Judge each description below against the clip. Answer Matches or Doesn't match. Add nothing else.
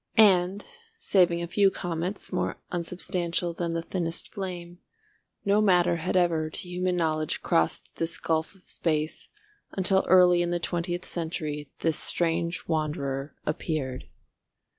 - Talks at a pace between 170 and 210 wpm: Doesn't match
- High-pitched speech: Doesn't match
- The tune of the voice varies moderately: Doesn't match